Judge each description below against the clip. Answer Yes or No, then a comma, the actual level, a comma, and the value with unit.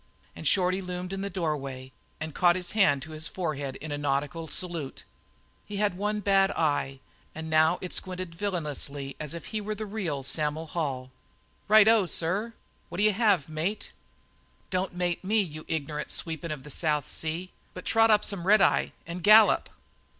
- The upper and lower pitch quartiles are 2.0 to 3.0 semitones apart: No, average, 4.5 semitones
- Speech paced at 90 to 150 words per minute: No, average, 175 wpm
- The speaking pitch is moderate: Yes, medium, 175 Hz